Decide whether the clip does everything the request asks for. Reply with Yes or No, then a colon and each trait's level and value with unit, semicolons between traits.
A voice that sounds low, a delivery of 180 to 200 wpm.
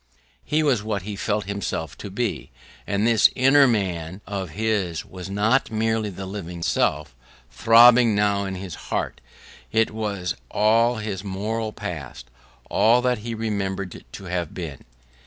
No: low, 105 Hz; average, 150 wpm